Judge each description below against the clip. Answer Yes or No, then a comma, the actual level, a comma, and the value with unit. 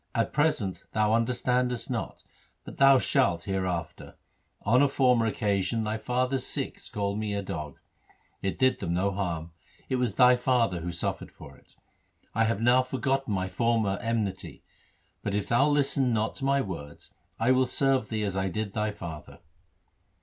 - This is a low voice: Yes, low, 110 Hz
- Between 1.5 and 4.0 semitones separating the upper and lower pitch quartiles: No, average, 4.6 semitones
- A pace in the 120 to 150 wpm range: No, average, 170 wpm